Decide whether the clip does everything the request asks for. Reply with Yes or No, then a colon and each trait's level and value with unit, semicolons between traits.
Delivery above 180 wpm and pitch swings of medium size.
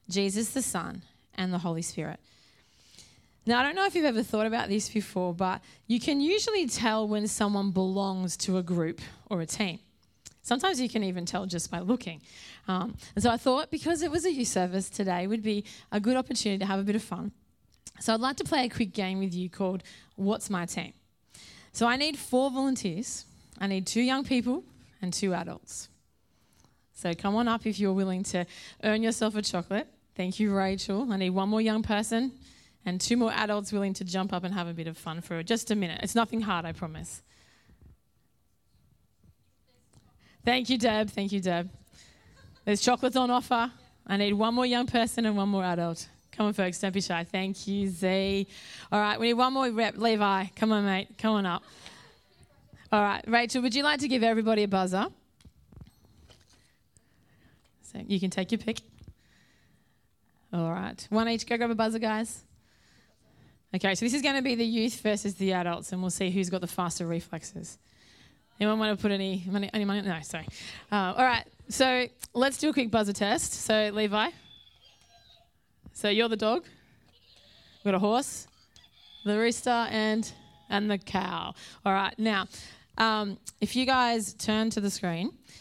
Yes: average, 190 wpm; average, 3.5 semitones